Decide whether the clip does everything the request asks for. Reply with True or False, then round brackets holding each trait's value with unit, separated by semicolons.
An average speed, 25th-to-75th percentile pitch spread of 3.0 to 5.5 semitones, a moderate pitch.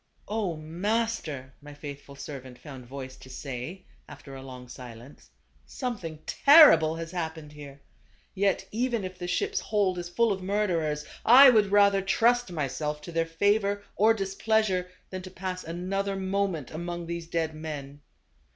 True (160 wpm; 5.2 semitones; 175 Hz)